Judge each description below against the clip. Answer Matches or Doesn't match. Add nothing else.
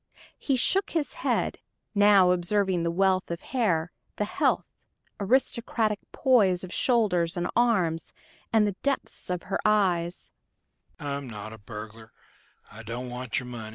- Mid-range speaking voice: Doesn't match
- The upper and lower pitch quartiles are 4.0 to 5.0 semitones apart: Matches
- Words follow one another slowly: Matches